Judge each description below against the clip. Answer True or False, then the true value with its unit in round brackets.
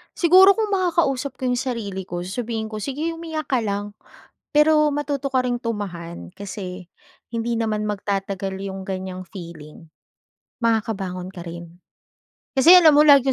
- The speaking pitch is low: False (220 Hz)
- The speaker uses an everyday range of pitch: False (6.7 semitones)